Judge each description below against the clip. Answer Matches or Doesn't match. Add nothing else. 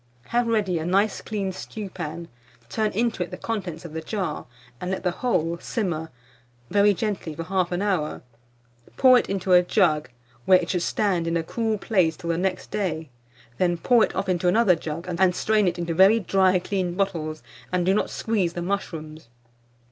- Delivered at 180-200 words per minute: Matches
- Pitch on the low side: Doesn't match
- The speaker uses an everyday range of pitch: Matches